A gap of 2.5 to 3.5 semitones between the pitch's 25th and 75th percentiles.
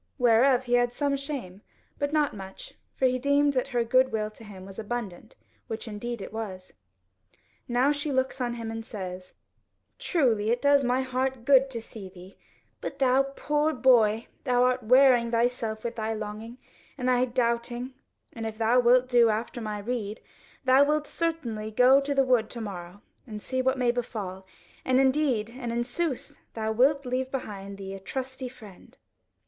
Yes: average, 3.2 semitones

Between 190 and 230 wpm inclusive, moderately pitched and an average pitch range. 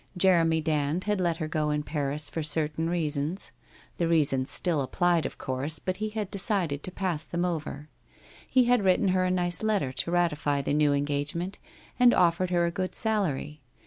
Yes: average, 195 wpm; medium, 165 Hz; average, 3.7 semitones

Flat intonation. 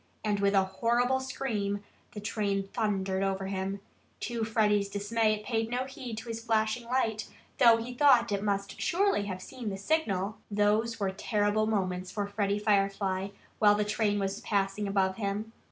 Yes: narrow, 2.3 semitones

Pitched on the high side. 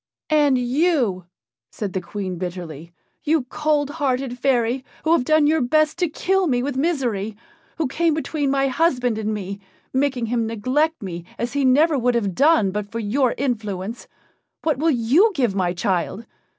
Yes: very high, 250 Hz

